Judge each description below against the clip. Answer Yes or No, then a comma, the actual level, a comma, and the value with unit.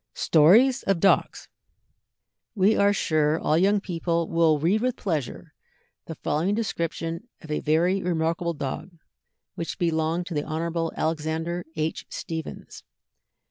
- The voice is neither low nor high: Yes, medium, 165 Hz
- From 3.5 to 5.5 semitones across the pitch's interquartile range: No, average, 2.8 semitones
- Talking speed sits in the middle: No, slow, 130 wpm